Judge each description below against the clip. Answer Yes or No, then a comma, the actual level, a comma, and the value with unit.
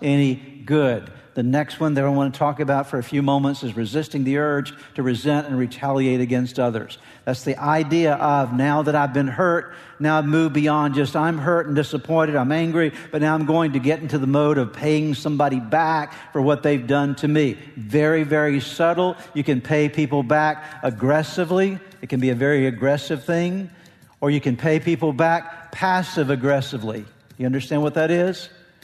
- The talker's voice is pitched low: No, medium, 150 Hz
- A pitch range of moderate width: No, narrow, 2.3 semitones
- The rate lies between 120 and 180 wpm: No, average, 195 wpm